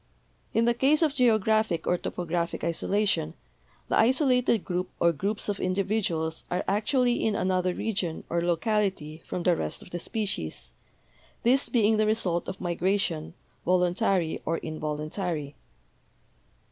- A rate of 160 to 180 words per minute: No, slow, 135 wpm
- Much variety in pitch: No, average, 4.4 semitones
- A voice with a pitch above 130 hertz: Yes, medium, 185 Hz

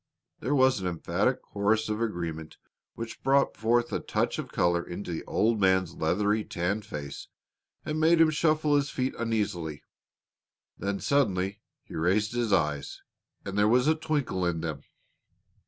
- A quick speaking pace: No, average, 155 wpm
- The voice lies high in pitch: No, low, 105 Hz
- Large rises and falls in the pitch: Yes, wide, 6.4 semitones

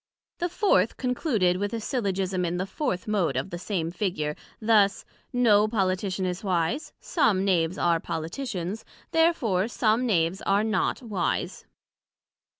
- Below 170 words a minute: Yes, average, 140 wpm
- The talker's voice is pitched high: Yes, high, 195 Hz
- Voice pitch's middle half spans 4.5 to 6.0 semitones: No, average, 4.1 semitones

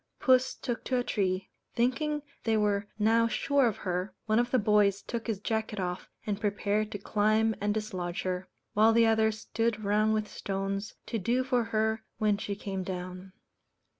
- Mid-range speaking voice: No, high, 215 Hz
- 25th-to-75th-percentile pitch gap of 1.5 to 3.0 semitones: Yes, narrow, 2.4 semitones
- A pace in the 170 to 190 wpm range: Yes, average, 180 wpm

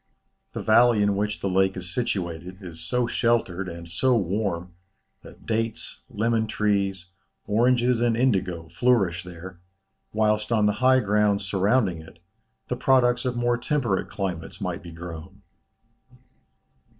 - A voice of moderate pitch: No, low, 105 Hz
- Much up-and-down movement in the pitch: No, average, 4.6 semitones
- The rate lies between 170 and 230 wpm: No, average, 140 wpm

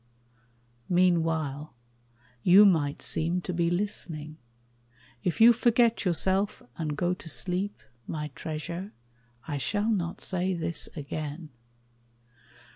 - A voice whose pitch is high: No, medium, 175 Hz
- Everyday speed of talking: No, slow, 110 wpm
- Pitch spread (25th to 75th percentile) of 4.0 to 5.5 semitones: No, average, 3.5 semitones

